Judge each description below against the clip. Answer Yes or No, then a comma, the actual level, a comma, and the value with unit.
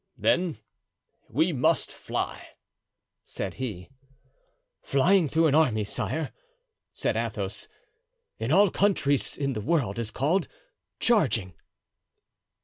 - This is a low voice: No, medium, 145 Hz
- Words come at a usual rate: No, slow, 105 wpm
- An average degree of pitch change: No, wide, 6.4 semitones